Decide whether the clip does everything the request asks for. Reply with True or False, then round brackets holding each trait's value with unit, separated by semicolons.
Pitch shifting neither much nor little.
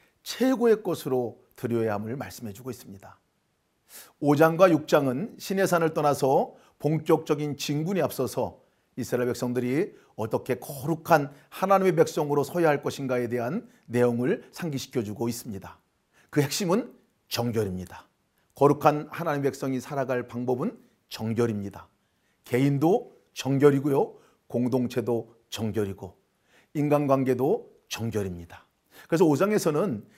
True (4.5 semitones)